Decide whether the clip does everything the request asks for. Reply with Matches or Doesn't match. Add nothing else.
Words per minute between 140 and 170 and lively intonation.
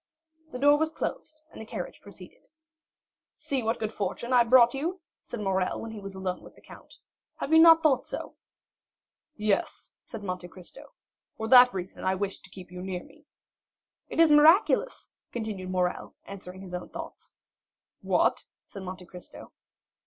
Matches